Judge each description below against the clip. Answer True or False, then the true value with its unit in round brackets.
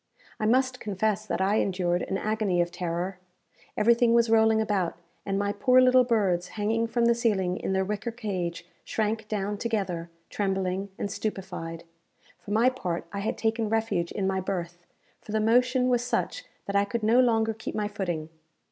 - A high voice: True (210 Hz)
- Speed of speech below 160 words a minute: False (180 wpm)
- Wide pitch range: False (3.2 semitones)